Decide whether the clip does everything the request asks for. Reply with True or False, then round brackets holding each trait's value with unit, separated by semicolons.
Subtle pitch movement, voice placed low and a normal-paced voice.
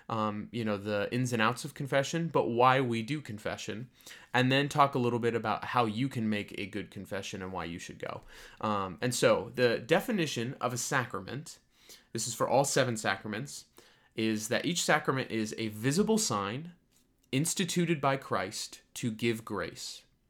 False (4.2 semitones; 120 Hz; 180 wpm)